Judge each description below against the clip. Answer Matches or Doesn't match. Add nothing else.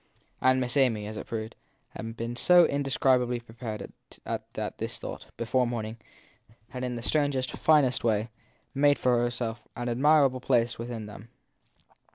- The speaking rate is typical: Matches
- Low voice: Matches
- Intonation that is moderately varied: Doesn't match